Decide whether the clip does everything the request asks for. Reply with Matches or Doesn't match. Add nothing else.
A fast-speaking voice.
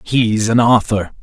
Doesn't match